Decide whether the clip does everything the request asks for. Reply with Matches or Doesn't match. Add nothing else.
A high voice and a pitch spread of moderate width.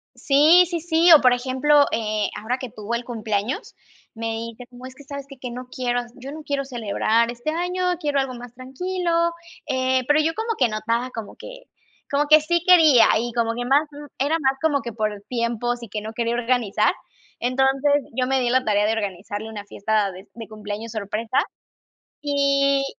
Matches